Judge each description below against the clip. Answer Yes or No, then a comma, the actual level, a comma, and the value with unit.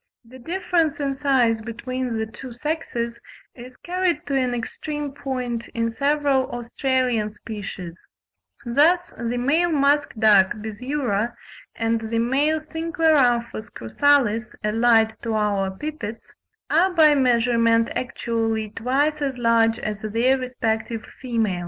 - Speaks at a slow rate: Yes, slow, 120 wpm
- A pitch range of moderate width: Yes, average, 4.1 semitones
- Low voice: No, high, 245 Hz